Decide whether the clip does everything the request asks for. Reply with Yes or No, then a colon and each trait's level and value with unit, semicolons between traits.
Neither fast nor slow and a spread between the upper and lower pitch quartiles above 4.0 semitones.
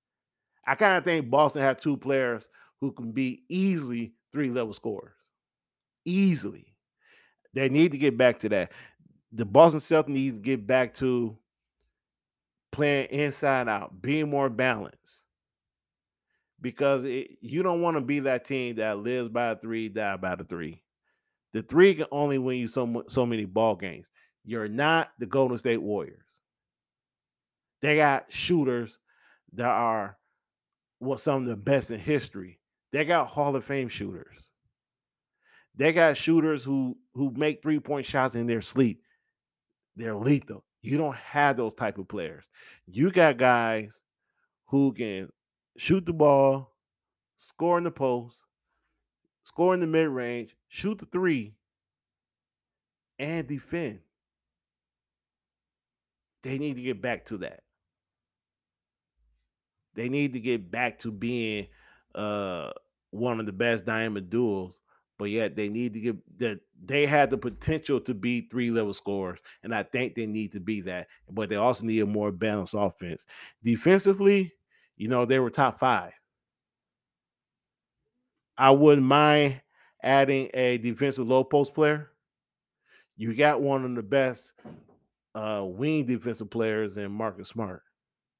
Yes: average, 145 wpm; average, 4.4 semitones